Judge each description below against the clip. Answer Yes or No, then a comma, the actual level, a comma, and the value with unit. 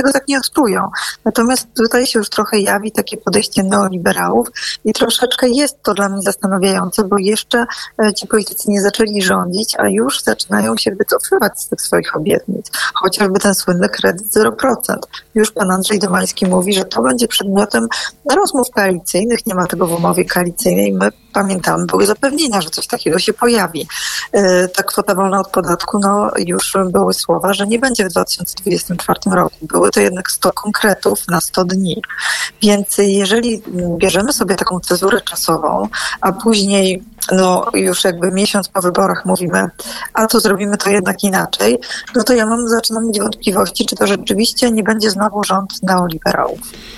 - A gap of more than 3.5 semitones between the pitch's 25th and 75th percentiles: No, average, 2.9 semitones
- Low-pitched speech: No, high, 205 Hz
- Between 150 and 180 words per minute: Yes, fast, 160 wpm